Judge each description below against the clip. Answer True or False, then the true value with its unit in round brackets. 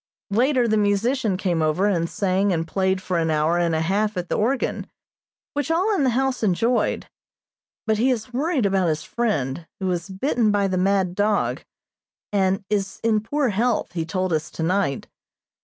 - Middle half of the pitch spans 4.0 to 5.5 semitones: True (4.5 semitones)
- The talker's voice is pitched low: False (200 Hz)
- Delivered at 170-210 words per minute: True (180 wpm)